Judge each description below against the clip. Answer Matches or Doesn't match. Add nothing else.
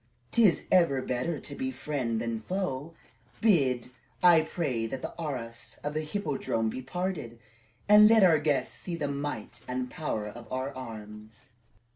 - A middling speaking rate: Matches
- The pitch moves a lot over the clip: Matches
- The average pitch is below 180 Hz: Matches